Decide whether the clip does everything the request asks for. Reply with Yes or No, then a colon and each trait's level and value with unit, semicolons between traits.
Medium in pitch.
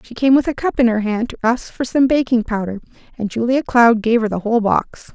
No: high, 235 Hz